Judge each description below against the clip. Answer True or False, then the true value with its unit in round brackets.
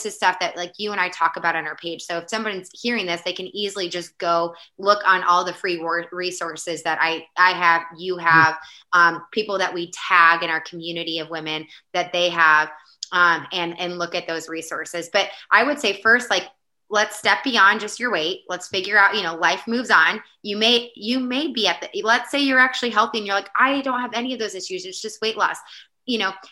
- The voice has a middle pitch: True (180 Hz)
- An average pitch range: True (3.9 semitones)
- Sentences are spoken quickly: True (235 wpm)